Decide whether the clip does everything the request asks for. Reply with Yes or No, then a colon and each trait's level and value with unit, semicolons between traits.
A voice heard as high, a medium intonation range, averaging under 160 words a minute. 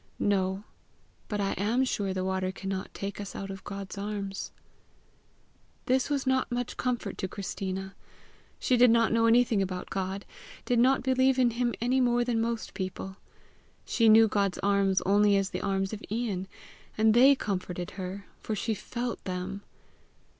No: high, 205 Hz; average, 3.7 semitones; average, 165 wpm